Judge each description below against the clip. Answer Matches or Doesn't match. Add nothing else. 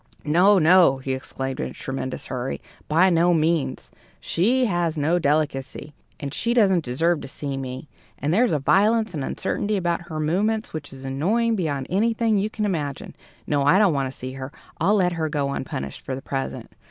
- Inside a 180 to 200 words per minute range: Matches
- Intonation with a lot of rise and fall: Matches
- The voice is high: Doesn't match